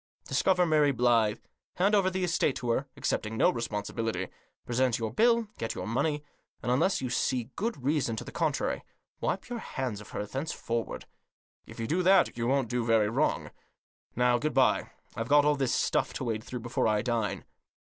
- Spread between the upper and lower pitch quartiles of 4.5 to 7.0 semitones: Yes, average, 4.9 semitones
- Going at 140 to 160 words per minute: No, average, 195 wpm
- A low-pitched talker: Yes, low, 125 Hz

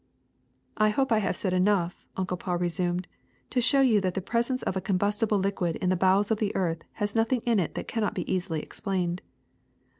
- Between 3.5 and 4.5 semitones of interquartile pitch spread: No, average, 3.1 semitones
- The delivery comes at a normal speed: No, fast, 215 wpm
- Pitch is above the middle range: Yes, high, 195 Hz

